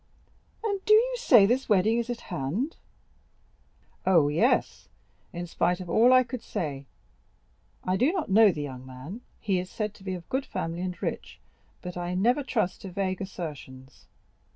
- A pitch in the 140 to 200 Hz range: Yes, high, 190 Hz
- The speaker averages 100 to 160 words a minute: No, average, 175 wpm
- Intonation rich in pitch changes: Yes, wide, 5.7 semitones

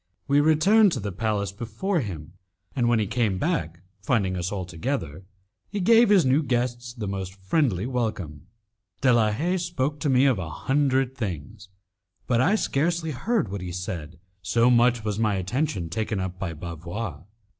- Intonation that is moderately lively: No, wide, 6.7 semitones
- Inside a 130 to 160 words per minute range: No, average, 175 wpm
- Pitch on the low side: Yes, low, 115 Hz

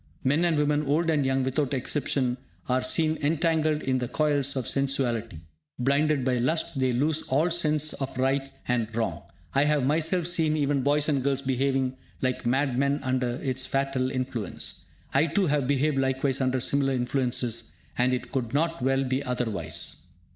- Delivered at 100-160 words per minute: No, average, 170 wpm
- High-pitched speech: No, low, 135 Hz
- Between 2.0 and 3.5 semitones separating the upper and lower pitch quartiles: Yes, narrow, 2.6 semitones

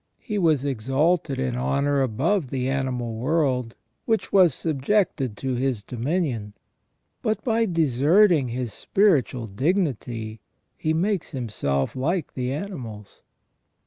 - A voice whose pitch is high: No, low, 135 Hz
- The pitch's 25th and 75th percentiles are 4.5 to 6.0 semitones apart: Yes, wide, 5.5 semitones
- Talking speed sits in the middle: No, slow, 115 wpm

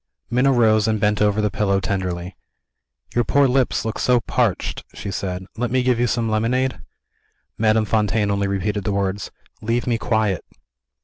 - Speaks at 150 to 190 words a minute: Yes, average, 170 wpm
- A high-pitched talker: No, low, 110 Hz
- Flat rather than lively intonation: No, average, 3.1 semitones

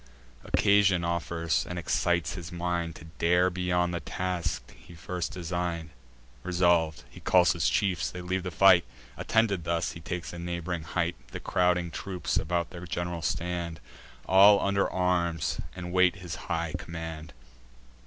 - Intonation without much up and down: Yes, narrow, 1.4 semitones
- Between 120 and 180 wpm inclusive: Yes, average, 150 wpm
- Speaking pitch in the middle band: No, very low, 85 Hz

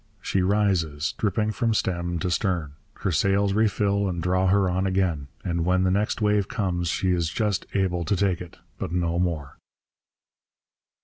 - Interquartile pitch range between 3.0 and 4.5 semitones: No, narrow, 2.6 semitones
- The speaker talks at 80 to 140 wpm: No, average, 170 wpm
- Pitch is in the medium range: No, very low, 95 Hz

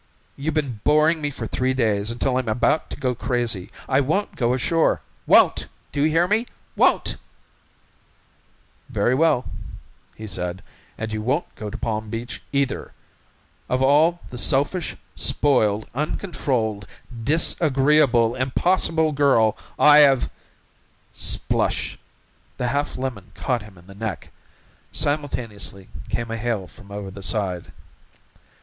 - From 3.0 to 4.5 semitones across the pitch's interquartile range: No, average, 5.0 semitones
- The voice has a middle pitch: No, low, 125 Hz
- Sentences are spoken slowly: Yes, slow, 130 wpm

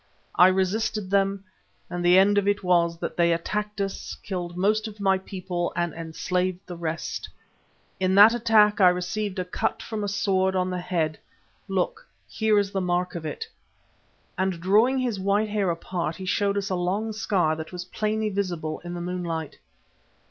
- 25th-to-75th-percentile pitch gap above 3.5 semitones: No, narrow, 2.5 semitones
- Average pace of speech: Yes, average, 180 wpm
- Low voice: No, medium, 185 Hz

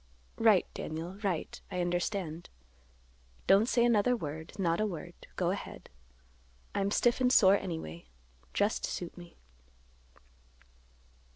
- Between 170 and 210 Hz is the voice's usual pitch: Yes, medium, 185 Hz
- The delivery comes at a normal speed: No, slow, 115 wpm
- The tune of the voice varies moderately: Yes, average, 3.8 semitones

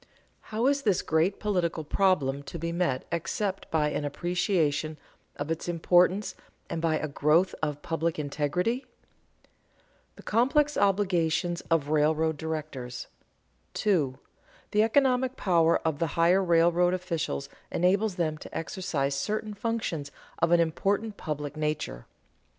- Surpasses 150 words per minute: No, slow, 135 wpm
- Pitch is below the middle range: No, medium, 170 Hz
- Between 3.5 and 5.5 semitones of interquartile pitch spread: Yes, average, 4.2 semitones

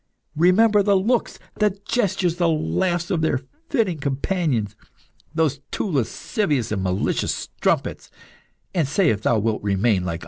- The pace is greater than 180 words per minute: No, average, 150 wpm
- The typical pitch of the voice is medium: Yes, medium, 160 Hz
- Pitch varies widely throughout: Yes, wide, 8.5 semitones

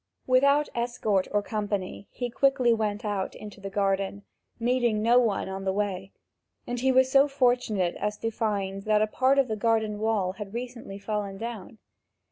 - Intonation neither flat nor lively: Yes, average, 3.4 semitones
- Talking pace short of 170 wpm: No, average, 175 wpm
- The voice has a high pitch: Yes, high, 215 Hz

